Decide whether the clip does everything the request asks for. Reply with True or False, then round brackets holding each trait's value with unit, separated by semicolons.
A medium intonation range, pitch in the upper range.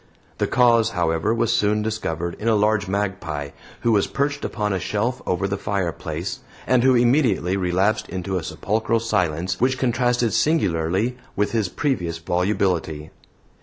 False (4.7 semitones; 105 Hz)